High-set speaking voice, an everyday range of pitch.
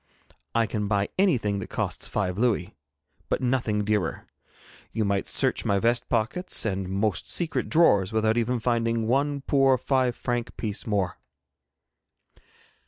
No: low, 115 Hz; average, 3.5 semitones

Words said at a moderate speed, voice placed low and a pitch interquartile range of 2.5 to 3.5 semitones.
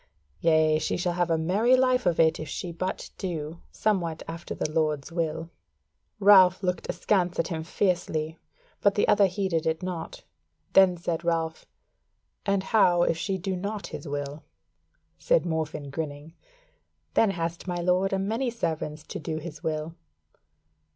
No: average, 155 wpm; medium, 170 Hz; average, 3.1 semitones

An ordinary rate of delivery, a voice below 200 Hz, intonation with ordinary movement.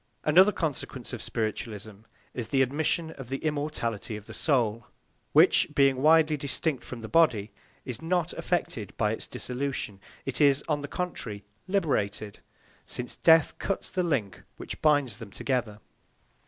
No: average, 150 wpm; low, 135 Hz; wide, 5.8 semitones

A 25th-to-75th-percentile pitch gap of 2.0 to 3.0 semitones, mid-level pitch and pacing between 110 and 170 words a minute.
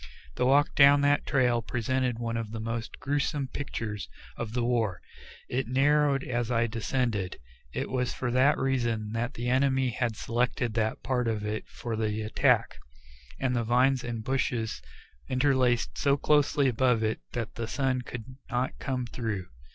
No: narrow, 2.6 semitones; low, 125 Hz; average, 160 wpm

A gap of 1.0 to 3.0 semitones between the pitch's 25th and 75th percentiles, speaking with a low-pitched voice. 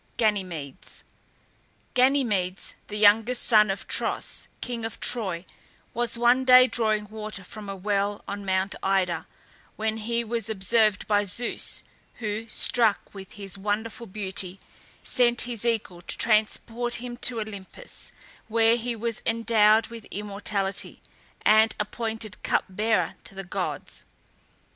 No: average, 2.7 semitones; high, 215 Hz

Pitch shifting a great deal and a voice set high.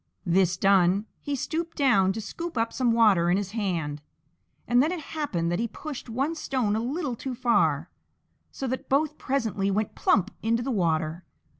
Yes: wide, 6.0 semitones; high, 230 Hz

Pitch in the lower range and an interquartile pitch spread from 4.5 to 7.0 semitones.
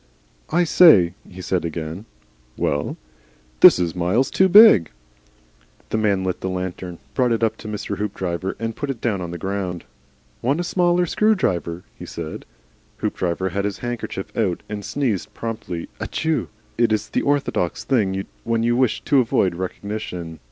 Yes: low, 100 Hz; average, 5.2 semitones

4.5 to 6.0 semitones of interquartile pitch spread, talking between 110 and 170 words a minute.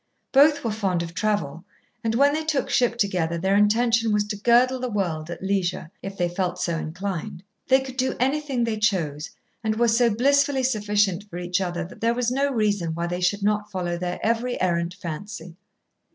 No: average, 5.1 semitones; average, 195 wpm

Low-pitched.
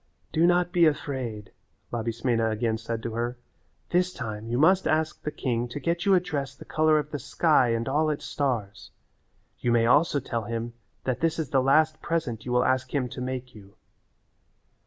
Yes: low, 130 Hz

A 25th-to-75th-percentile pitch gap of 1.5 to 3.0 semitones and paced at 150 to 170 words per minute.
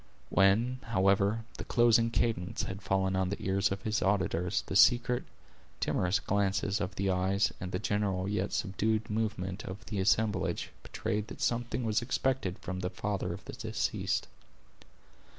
Yes: average, 2.7 semitones; average, 160 wpm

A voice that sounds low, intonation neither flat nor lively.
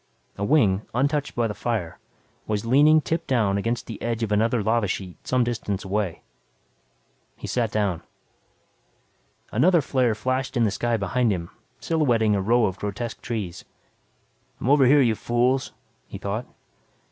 Yes: low, 115 Hz; average, 3.8 semitones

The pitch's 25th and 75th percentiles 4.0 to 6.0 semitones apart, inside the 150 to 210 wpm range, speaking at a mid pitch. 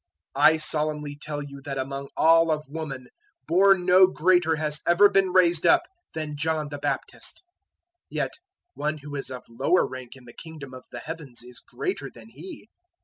No: average, 3.3 semitones; average, 180 wpm; medium, 150 Hz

